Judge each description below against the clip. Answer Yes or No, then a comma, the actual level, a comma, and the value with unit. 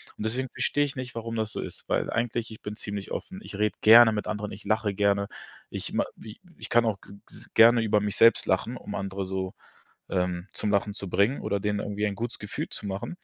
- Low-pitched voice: Yes, low, 105 Hz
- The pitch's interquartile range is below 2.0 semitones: No, narrow, 2.4 semitones